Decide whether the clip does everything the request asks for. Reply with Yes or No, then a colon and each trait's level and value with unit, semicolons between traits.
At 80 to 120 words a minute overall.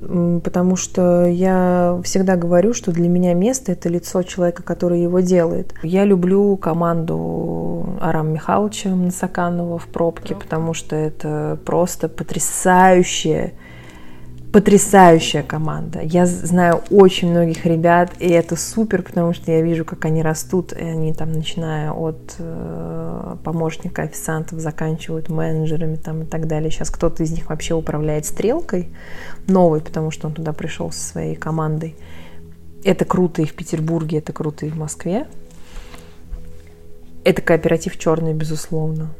No: average, 135 wpm